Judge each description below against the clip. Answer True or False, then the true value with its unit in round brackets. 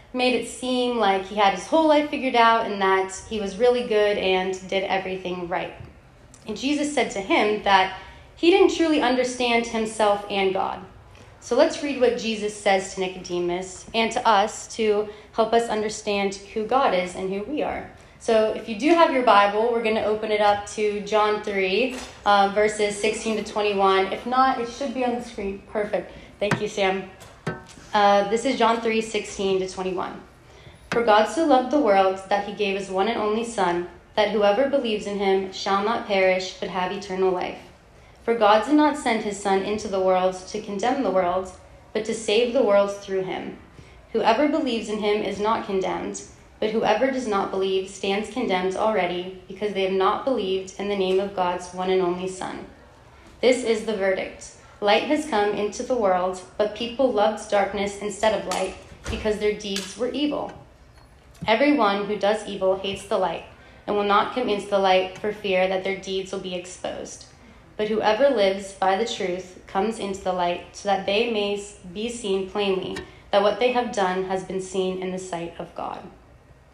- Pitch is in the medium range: False (205 Hz)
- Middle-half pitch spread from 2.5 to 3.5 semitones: True (2.8 semitones)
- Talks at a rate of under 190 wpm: False (195 wpm)